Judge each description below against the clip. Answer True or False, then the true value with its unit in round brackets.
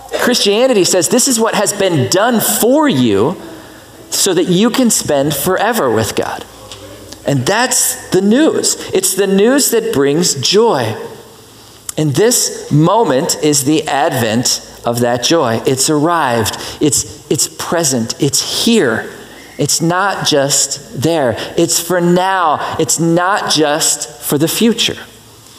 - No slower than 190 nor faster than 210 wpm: False (135 wpm)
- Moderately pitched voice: True (165 Hz)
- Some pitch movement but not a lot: False (6.4 semitones)